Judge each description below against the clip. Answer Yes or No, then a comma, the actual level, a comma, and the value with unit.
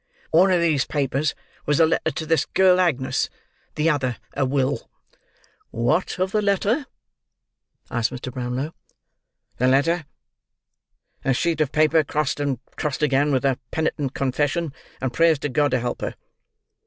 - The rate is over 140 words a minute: Yes, average, 150 wpm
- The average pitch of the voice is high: No, medium, 145 Hz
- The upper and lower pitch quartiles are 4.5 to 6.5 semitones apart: No, average, 3.7 semitones